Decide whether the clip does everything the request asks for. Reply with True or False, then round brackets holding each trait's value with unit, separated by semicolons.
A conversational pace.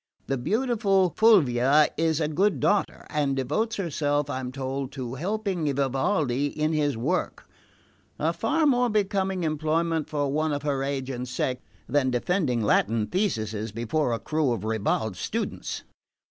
True (145 wpm)